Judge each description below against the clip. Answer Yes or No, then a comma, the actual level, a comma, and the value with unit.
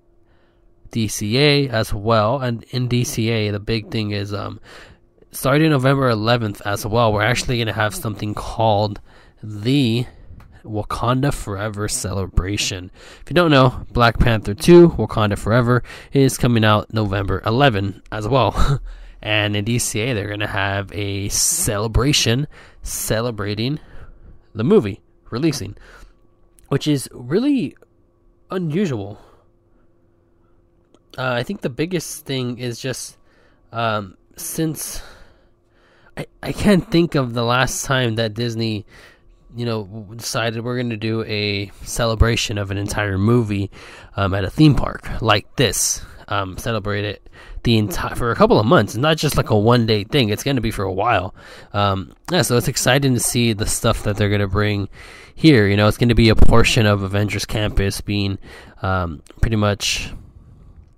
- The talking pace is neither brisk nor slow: Yes, average, 150 wpm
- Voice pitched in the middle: No, low, 110 Hz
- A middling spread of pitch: Yes, average, 3.5 semitones